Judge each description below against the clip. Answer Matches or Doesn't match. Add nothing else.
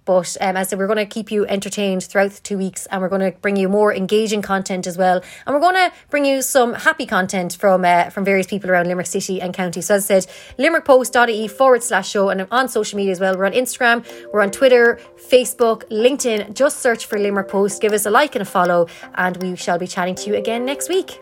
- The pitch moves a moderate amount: Matches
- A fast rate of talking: Matches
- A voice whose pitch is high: Matches